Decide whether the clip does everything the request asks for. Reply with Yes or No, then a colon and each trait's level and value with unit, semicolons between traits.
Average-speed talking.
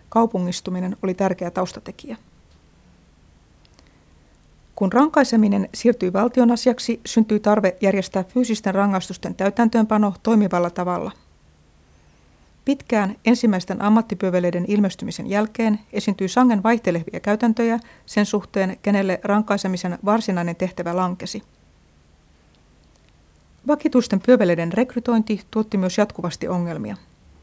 No: slow, 90 wpm